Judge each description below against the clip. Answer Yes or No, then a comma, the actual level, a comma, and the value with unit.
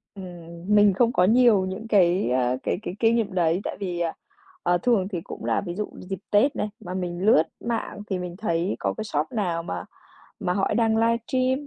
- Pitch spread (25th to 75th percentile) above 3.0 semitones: Yes, average, 4.0 semitones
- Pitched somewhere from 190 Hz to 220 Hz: Yes, high, 195 Hz